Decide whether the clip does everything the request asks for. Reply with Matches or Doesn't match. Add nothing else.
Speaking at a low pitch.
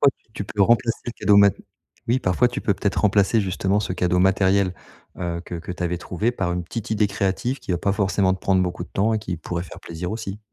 Matches